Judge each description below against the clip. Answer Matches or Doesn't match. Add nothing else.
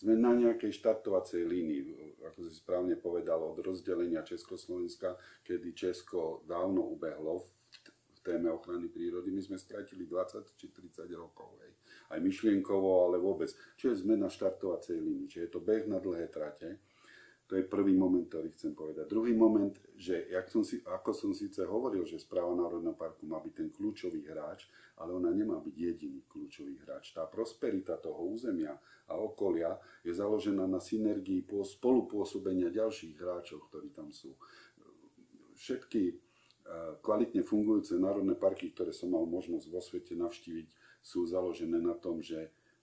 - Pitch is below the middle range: Doesn't match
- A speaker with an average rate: Matches